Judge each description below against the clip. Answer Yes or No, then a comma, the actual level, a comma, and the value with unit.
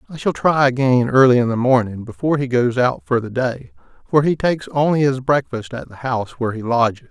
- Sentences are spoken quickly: Yes, fast, 230 wpm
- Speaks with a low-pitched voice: Yes, low, 125 Hz